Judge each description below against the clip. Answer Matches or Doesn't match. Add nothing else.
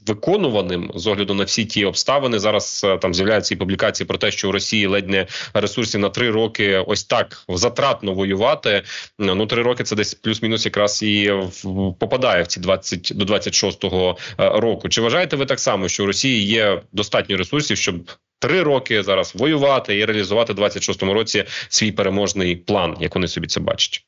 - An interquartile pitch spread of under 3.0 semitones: Matches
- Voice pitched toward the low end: Matches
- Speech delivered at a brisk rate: Matches